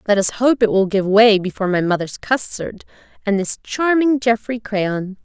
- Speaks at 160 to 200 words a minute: Yes, average, 185 wpm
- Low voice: No, high, 215 Hz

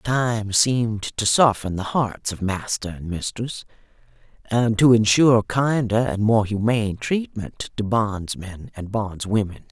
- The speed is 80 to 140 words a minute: Yes, slow, 135 wpm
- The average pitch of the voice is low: Yes, low, 110 Hz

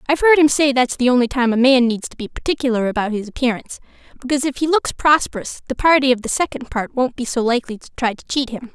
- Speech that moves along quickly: Yes, fast, 255 wpm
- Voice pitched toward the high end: Yes, very high, 255 Hz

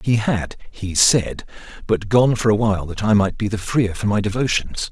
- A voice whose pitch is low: Yes, low, 105 Hz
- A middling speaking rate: No, fast, 220 wpm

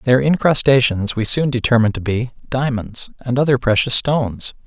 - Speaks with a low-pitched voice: Yes, low, 125 Hz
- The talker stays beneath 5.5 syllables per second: Yes, 5.2 syllables/s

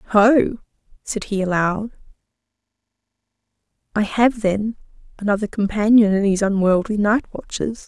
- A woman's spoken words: Yes, female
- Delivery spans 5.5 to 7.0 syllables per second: No, 4.7 syllables/s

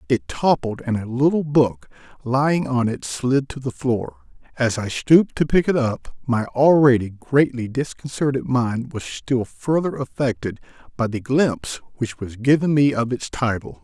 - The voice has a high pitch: No, low, 125 Hz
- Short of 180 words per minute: Yes, average, 170 wpm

